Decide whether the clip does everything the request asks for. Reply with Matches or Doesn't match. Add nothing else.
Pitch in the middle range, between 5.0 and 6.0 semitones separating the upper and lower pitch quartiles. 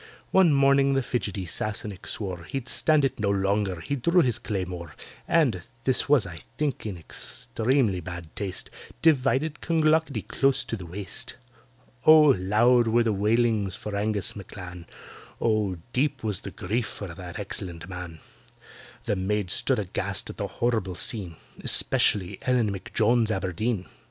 Doesn't match